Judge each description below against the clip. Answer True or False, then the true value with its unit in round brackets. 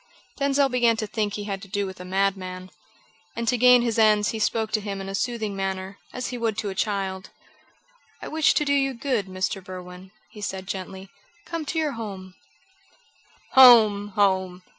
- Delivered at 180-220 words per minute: True (190 wpm)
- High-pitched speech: True (205 Hz)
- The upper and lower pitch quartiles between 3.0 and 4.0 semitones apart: True (3.6 semitones)